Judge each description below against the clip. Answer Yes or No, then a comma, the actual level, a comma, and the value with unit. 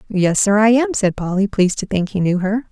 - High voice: Yes, high, 200 Hz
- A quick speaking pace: Yes, fast, 265 wpm